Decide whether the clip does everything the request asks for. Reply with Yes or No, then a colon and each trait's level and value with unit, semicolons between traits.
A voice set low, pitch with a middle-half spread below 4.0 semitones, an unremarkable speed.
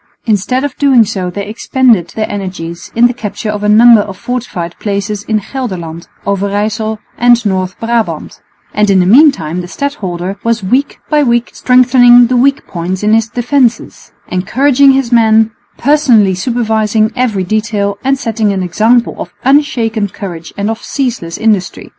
No: high, 220 Hz; average, 3.6 semitones; average, 160 wpm